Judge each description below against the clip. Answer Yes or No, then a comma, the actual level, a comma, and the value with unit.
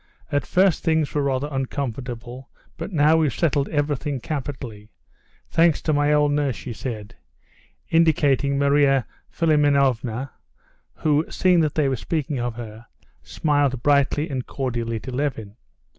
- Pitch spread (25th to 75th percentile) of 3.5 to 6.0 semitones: No, average, 2.9 semitones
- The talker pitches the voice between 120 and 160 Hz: Yes, medium, 140 Hz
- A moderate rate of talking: No, slow, 130 wpm